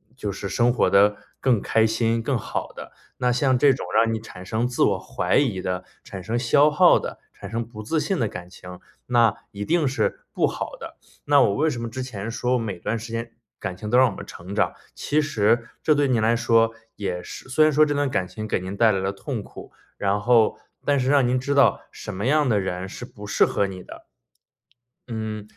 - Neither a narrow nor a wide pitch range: Yes, average, 4.1 semitones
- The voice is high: No, low, 115 Hz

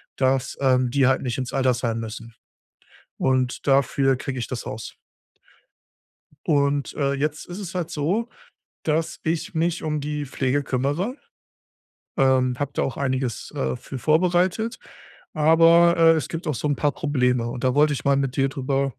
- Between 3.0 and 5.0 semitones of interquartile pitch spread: Yes, average, 3.5 semitones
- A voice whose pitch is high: No, medium, 140 Hz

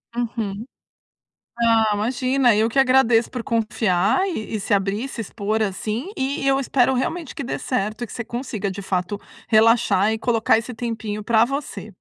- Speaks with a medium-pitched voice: No, high, 230 Hz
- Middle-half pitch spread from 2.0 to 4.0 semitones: Yes, average, 3.0 semitones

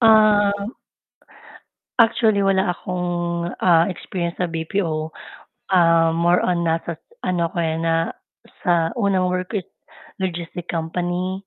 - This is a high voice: No, medium, 175 Hz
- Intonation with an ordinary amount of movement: No, narrow, 2.3 semitones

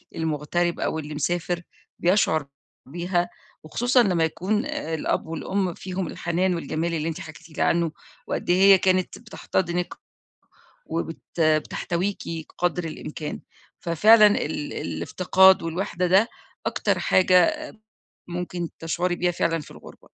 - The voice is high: No, medium, 175 Hz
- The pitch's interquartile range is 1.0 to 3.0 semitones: Yes, narrow, 2.5 semitones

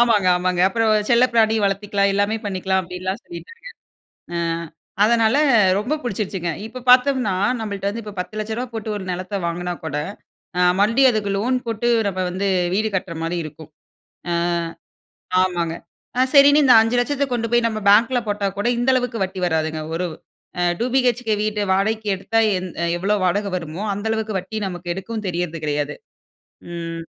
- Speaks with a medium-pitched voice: No, high, 205 Hz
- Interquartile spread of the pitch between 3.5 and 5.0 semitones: Yes, average, 4.0 semitones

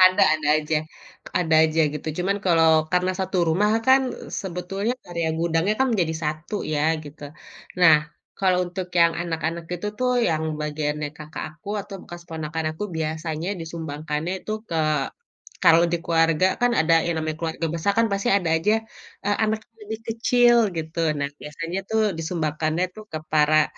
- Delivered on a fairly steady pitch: No, average, 3.0 semitones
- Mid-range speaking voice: Yes, medium, 165 Hz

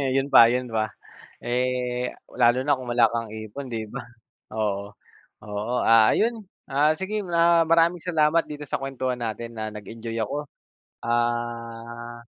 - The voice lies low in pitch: Yes, low, 120 Hz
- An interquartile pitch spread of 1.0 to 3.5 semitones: No, average, 4.2 semitones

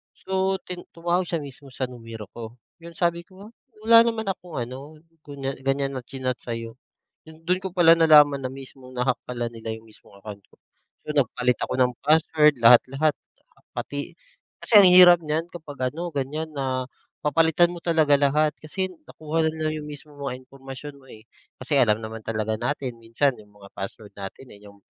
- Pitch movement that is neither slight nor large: Yes, average, 4.6 semitones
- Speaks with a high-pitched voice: No, medium, 140 Hz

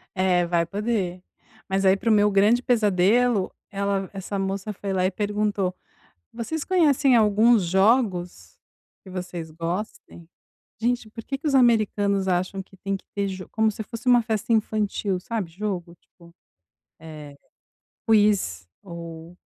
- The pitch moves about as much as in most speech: Yes, average, 3.4 semitones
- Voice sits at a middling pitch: No, high, 200 Hz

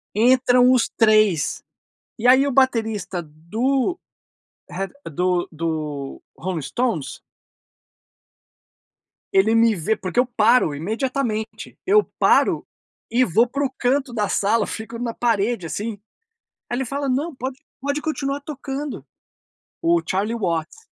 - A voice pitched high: Yes, high, 230 Hz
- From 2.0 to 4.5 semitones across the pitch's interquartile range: No, average, 5.2 semitones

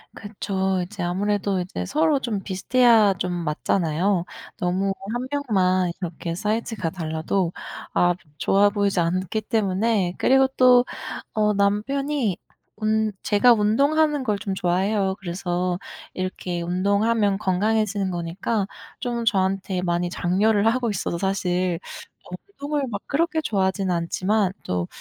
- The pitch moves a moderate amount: Yes, average, 3.4 semitones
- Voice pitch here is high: Yes, high, 200 Hz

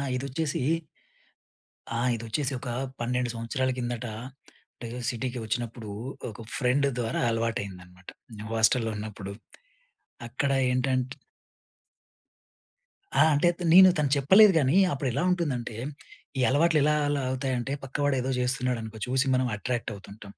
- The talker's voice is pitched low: Yes, low, 125 Hz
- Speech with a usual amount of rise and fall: Yes, average, 3.3 semitones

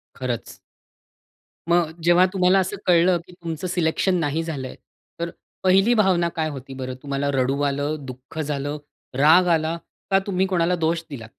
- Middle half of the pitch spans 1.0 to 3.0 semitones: No, average, 4.2 semitones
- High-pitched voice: No, medium, 160 Hz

